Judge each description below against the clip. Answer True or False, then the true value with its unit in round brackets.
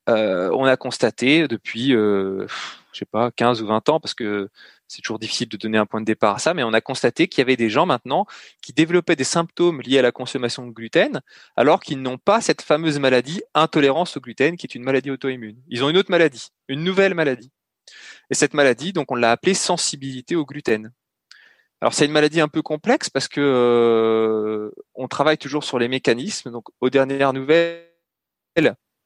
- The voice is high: False (135 Hz)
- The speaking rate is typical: True (205 wpm)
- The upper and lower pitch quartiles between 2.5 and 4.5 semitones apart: False (5.0 semitones)